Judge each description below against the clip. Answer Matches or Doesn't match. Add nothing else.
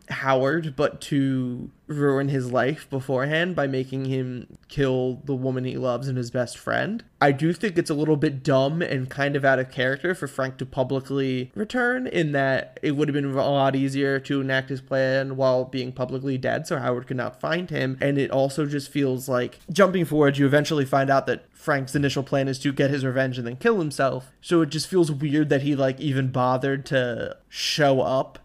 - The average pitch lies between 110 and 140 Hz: Matches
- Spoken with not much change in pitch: Matches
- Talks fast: Matches